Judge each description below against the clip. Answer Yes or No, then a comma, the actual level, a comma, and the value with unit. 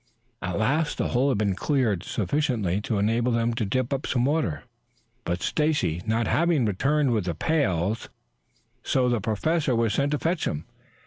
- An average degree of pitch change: No, wide, 5.8 semitones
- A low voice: Yes, low, 120 Hz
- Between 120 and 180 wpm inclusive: Yes, average, 170 wpm